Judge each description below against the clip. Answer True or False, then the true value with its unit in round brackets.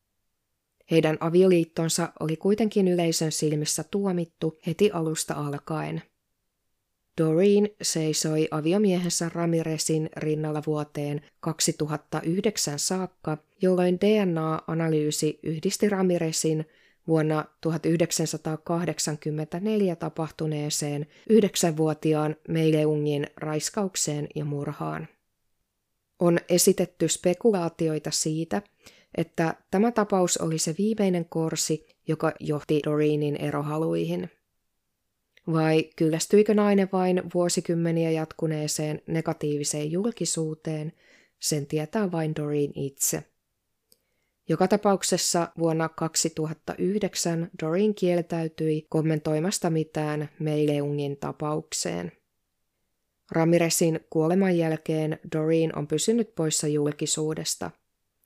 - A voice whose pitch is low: False (160 Hz)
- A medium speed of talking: False (80 wpm)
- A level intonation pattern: True (2.3 semitones)